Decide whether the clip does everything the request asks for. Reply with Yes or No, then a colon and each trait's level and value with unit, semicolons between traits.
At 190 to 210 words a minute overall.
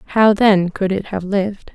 Yes: fast, 205 wpm